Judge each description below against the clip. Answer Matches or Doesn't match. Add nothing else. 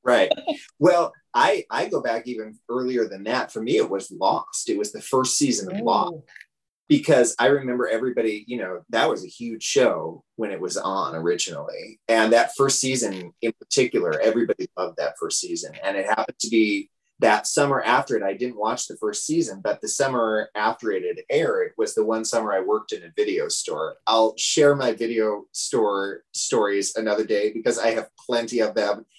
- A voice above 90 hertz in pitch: Matches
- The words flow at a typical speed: Matches